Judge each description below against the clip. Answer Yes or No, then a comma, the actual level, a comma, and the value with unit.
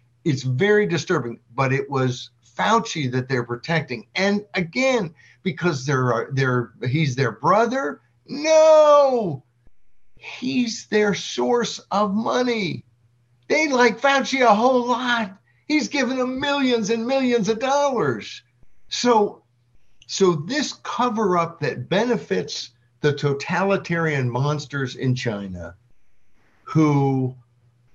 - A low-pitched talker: No, medium, 165 Hz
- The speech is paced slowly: Yes, slow, 105 wpm